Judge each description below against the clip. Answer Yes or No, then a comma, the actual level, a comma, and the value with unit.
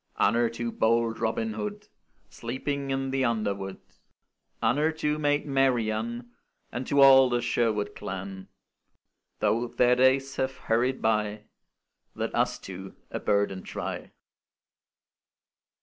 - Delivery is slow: Yes, slow, 120 wpm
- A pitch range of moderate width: Yes, average, 3.8 semitones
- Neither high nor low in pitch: No, low, 120 Hz